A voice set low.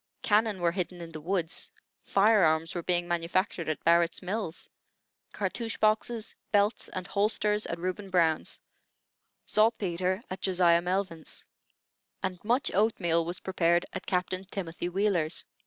No: medium, 185 Hz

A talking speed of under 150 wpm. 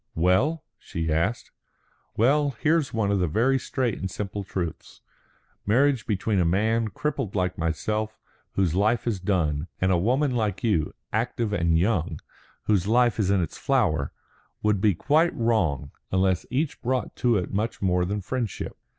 No: average, 160 wpm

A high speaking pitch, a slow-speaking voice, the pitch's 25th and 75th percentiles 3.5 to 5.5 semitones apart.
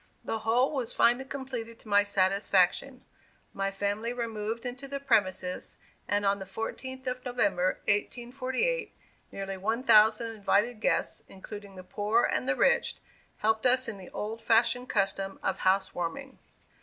No: high, 225 Hz; average, 150 wpm; average, 4.0 semitones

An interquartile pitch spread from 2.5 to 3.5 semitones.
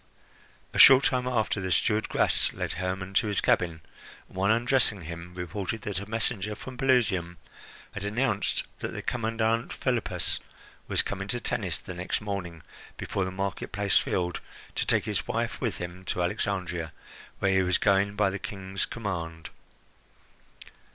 Yes: average, 3.2 semitones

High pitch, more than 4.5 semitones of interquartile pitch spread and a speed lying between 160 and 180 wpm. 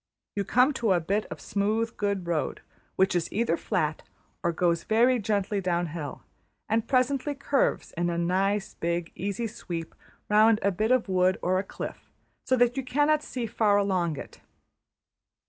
Yes: high, 200 Hz; average, 4.9 semitones; average, 170 wpm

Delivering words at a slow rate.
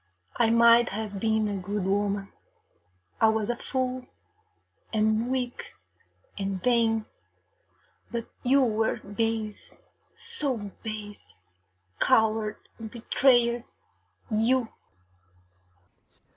Yes: slow, 90 wpm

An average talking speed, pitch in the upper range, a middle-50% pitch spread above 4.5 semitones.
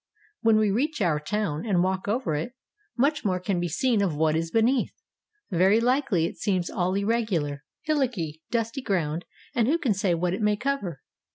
Yes: average, 185 wpm; high, 200 Hz; average, 5.3 semitones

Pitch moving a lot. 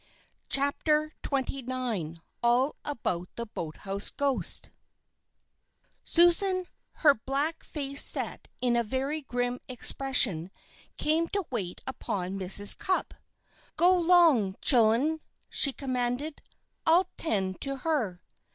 Yes: wide, 5.7 semitones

